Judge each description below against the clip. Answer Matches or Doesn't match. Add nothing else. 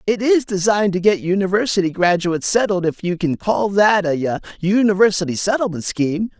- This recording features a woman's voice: Doesn't match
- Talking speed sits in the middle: Matches